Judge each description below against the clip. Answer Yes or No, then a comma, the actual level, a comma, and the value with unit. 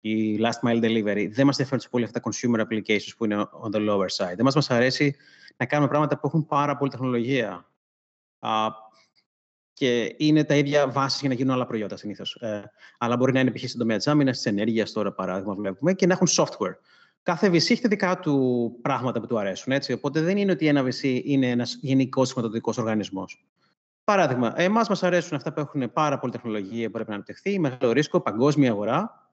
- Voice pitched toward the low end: Yes, low, 125 Hz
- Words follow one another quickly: Yes, fast, 205 wpm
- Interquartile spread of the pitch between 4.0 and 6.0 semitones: Yes, average, 5.0 semitones